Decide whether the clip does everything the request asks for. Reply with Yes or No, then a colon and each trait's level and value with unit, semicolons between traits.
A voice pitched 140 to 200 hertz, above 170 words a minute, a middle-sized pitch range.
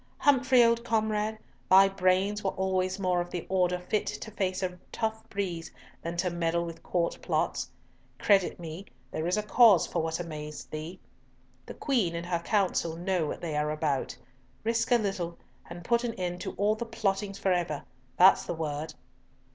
Yes: medium, 185 Hz; average, 180 wpm; average, 3.6 semitones